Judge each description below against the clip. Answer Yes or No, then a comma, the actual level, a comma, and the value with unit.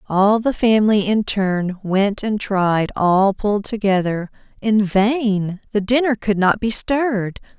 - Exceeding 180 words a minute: No, average, 150 wpm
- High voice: Yes, high, 205 Hz